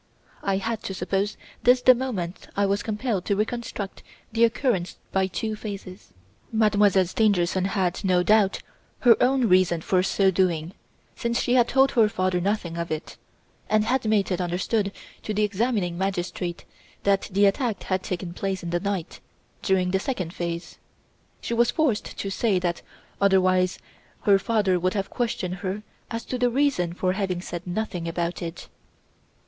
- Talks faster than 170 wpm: No, average, 165 wpm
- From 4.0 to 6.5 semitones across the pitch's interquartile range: No, average, 3.3 semitones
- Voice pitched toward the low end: No, high, 195 Hz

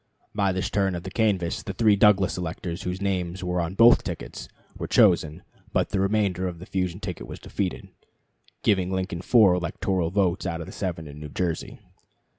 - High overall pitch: No, very low, 95 Hz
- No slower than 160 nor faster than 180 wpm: No, average, 190 wpm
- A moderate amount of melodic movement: No, narrow, 2.3 semitones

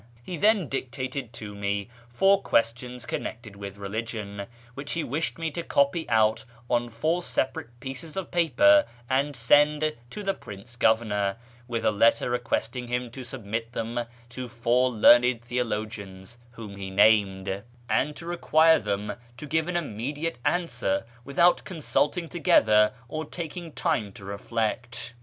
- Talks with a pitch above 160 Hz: No, low, 120 Hz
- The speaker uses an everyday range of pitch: No, wide, 6.0 semitones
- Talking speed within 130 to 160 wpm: Yes, average, 150 wpm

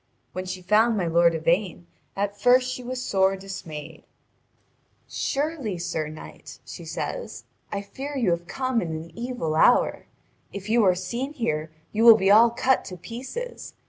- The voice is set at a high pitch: Yes, high, 200 Hz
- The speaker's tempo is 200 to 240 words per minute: No, average, 165 wpm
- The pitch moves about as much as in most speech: No, wide, 6.0 semitones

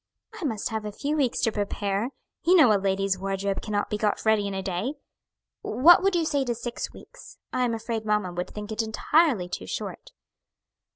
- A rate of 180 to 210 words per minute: Yes, fast, 205 wpm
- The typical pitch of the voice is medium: No, high, 220 Hz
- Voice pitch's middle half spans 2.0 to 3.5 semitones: No, average, 4.2 semitones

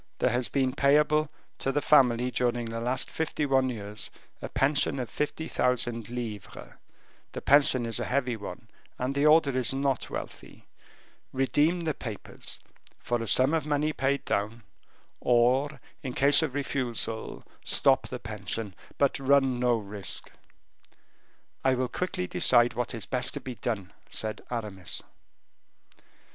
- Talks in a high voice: No, low, 125 Hz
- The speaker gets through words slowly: No, average, 150 wpm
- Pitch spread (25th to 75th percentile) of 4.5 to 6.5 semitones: No, average, 3.3 semitones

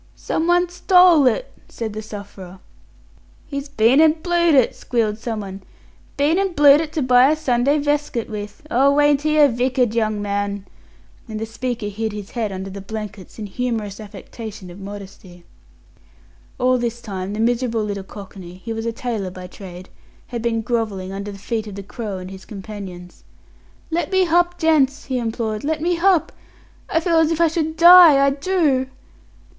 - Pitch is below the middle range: No, high, 235 Hz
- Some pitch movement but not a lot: No, wide, 6.4 semitones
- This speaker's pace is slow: No, average, 175 wpm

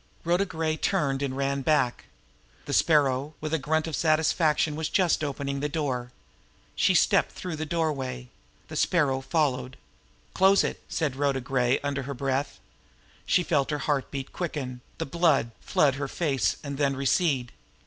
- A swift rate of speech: No, average, 160 wpm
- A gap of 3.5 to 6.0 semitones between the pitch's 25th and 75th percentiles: No, average, 2.9 semitones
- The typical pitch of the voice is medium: Yes, medium, 145 Hz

